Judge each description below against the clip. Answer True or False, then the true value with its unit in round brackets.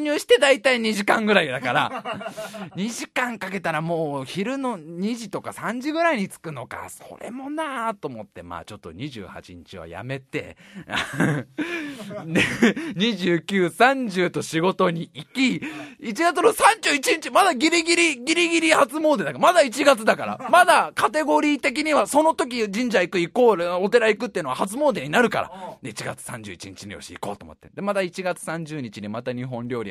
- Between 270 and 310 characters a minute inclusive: True (295 characters per minute)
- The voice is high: True (220 Hz)